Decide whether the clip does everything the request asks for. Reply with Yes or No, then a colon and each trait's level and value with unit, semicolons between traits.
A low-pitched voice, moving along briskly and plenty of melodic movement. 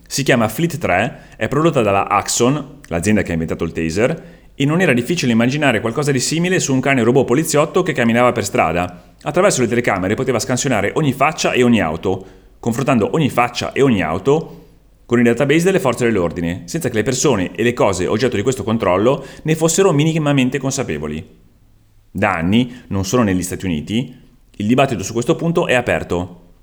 Yes: low, 125 Hz; fast, 185 wpm; wide, 6.0 semitones